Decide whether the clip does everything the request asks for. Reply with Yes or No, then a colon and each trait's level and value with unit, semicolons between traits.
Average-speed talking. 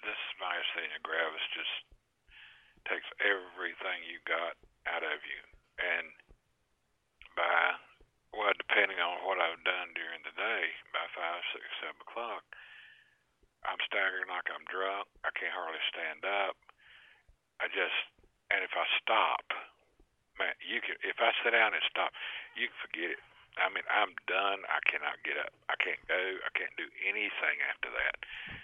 Yes: average, 155 wpm